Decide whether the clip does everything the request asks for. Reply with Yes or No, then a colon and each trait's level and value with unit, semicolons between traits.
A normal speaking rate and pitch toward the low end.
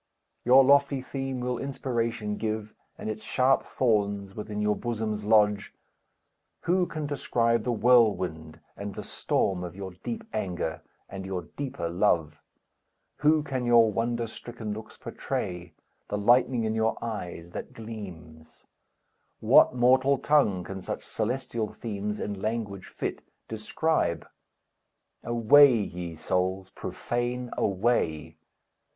No: slow, 125 wpm; low, 110 Hz